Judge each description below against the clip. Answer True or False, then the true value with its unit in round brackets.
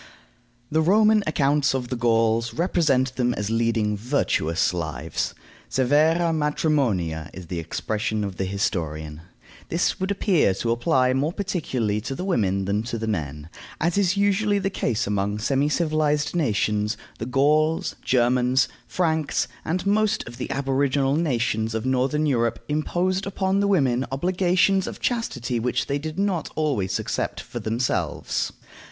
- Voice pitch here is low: True (130 Hz)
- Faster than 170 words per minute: False (145 wpm)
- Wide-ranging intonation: True (6.9 semitones)